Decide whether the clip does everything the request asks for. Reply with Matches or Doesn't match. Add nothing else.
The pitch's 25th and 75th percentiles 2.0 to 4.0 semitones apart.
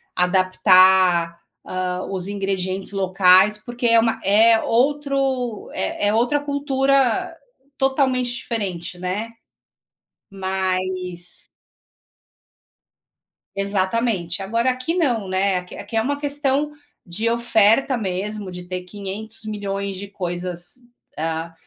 Doesn't match